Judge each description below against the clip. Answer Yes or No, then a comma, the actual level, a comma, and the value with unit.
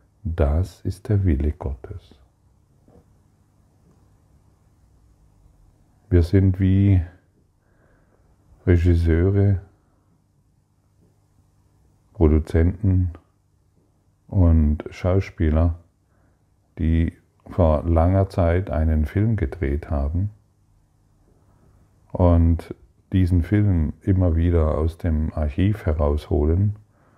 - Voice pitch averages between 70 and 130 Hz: Yes, very low, 95 Hz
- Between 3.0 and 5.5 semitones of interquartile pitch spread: Yes, average, 3.3 semitones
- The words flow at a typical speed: No, slow, 65 wpm